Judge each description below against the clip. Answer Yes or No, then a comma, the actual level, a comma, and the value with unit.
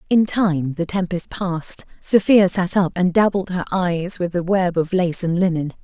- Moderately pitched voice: Yes, medium, 180 Hz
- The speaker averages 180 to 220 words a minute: Yes, average, 195 wpm